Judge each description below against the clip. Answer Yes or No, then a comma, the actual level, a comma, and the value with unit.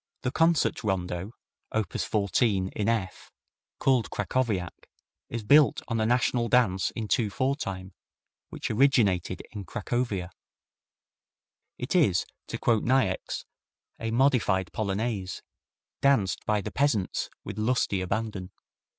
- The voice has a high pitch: No, low, 110 Hz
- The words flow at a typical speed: No, slow, 120 wpm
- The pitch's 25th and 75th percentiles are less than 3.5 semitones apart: No, average, 4.4 semitones